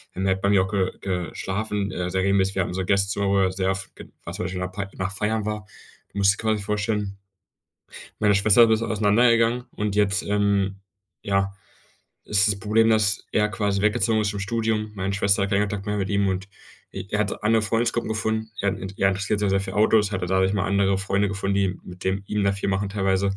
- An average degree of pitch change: No, narrow, 1.5 semitones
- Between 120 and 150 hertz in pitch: No, low, 100 Hz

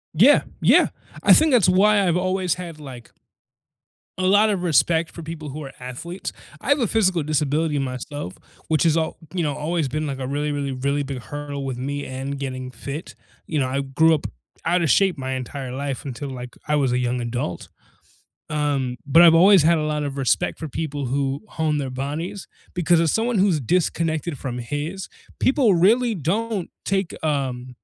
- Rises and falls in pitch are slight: No, average, 4.5 semitones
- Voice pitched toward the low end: No, medium, 150 Hz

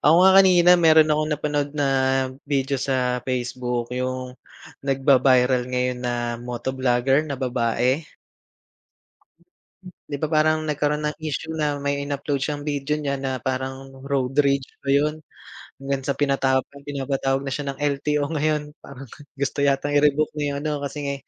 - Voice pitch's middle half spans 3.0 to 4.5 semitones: No, narrow, 2.4 semitones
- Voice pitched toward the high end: No, medium, 140 Hz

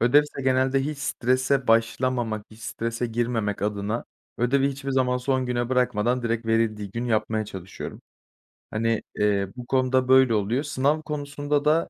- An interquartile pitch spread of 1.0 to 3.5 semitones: Yes, average, 2.9 semitones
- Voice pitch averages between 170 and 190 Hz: No, low, 125 Hz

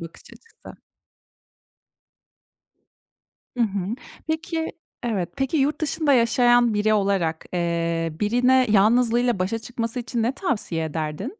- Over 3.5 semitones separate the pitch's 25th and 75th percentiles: Yes, average, 5.1 semitones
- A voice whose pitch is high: Yes, high, 230 Hz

